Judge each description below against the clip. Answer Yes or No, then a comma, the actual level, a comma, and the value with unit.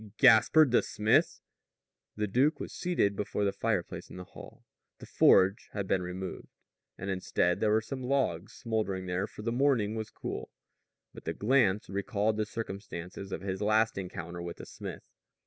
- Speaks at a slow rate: No, average, 170 wpm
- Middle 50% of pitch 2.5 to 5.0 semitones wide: Yes, average, 3.0 semitones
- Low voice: Yes, low, 105 Hz